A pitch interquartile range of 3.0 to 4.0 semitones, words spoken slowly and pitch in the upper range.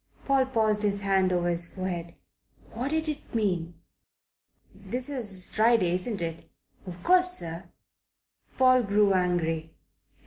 No: wide, 5.6 semitones; slow, 130 wpm; high, 195 Hz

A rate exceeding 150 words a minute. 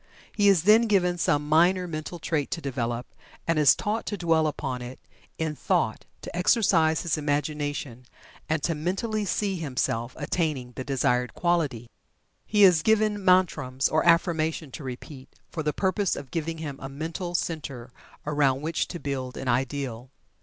Yes: average, 160 wpm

